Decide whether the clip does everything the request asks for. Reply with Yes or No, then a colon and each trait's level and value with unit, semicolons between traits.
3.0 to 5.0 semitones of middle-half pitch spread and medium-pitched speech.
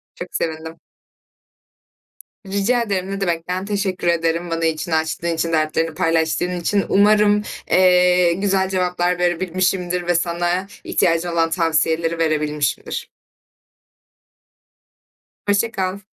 No: narrow, 2.4 semitones; medium, 175 Hz